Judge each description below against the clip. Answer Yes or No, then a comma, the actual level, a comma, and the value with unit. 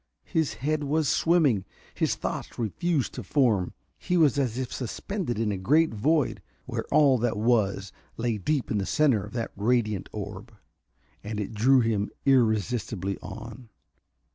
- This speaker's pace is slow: No, average, 155 wpm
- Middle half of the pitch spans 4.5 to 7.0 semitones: Yes, average, 5.3 semitones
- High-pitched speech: No, low, 120 Hz